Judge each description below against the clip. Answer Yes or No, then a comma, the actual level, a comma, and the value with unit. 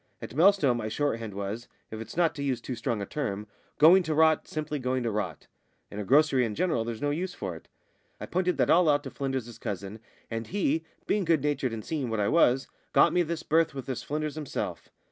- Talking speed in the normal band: No, fast, 225 wpm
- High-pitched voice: No, low, 135 Hz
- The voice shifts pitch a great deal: Yes, wide, 5.7 semitones